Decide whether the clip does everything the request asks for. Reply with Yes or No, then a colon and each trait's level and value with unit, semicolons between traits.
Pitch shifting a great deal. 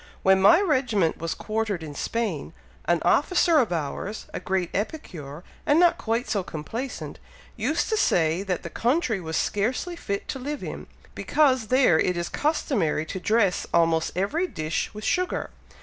Yes: wide, 8.0 semitones